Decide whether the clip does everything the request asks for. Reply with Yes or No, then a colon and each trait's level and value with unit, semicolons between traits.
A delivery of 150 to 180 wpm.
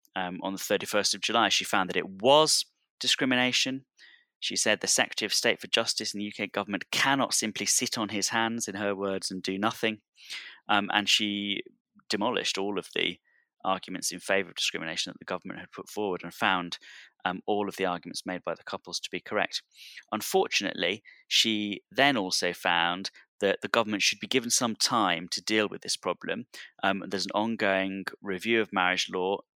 No: average, 190 wpm